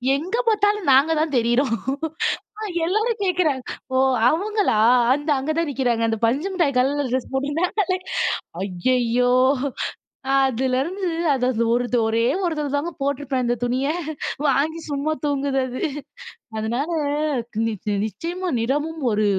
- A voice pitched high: Yes, very high, 280 Hz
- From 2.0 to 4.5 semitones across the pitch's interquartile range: No, average, 4.9 semitones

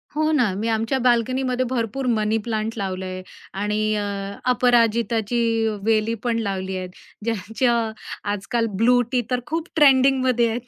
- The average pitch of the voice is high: Yes, high, 230 Hz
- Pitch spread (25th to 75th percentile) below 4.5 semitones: Yes, average, 2.8 semitones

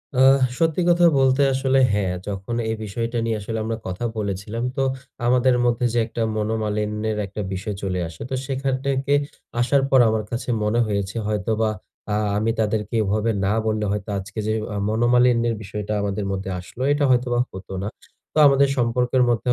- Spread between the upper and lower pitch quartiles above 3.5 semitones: No, average, 3.1 semitones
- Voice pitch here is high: No, low, 110 Hz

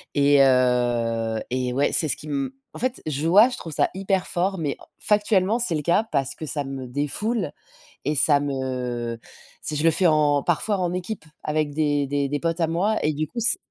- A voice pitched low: No, medium, 150 Hz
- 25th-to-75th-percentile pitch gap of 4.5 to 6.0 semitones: Yes, average, 4.9 semitones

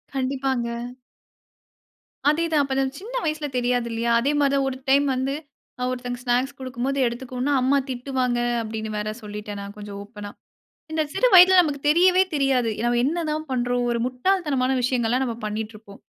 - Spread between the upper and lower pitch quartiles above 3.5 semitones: No, average, 3.0 semitones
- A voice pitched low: No, very high, 255 Hz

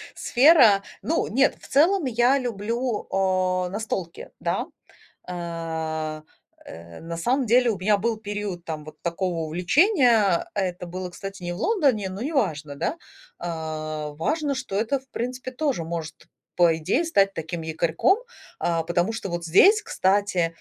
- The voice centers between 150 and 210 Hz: Yes, high, 190 Hz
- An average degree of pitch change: No, wide, 6.5 semitones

